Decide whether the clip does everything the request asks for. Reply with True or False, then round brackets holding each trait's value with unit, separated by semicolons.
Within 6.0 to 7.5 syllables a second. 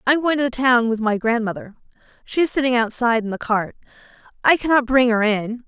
True (6.2 syllables/s)